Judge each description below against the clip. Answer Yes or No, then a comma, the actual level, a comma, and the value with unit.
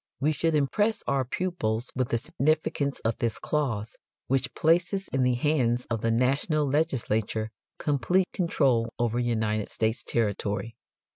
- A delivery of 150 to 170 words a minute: No, average, 140 wpm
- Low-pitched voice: Yes, low, 130 Hz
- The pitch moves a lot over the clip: No, average, 5.0 semitones